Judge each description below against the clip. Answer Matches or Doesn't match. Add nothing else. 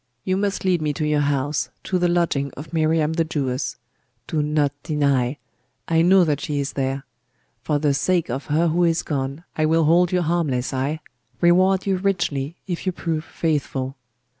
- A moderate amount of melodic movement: Matches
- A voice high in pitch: Doesn't match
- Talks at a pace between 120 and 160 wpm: Doesn't match